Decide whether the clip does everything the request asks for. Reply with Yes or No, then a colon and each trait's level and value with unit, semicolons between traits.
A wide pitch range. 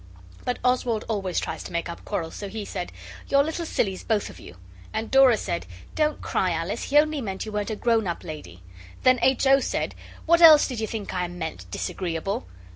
Yes: wide, 6.5 semitones